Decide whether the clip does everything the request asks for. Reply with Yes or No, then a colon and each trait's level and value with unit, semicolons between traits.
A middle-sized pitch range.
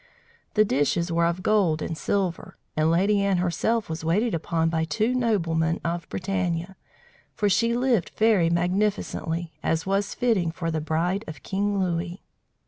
Yes: average, 3.7 semitones